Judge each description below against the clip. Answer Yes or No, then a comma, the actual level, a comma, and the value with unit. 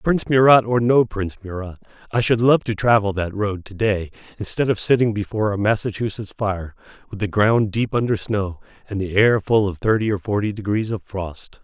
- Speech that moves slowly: No, average, 200 wpm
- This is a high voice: No, low, 105 Hz